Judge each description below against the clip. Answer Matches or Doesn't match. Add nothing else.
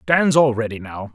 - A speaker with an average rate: Matches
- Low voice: Matches